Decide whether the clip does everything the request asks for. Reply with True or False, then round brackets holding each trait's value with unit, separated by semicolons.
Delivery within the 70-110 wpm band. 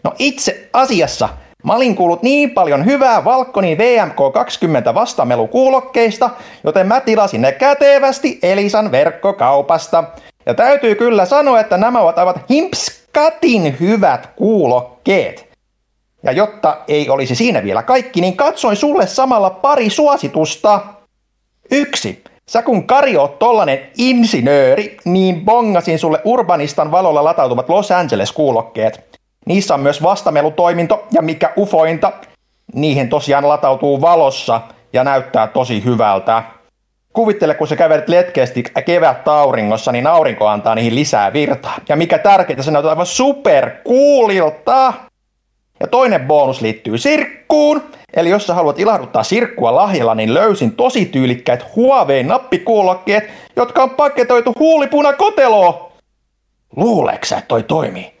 False (120 wpm)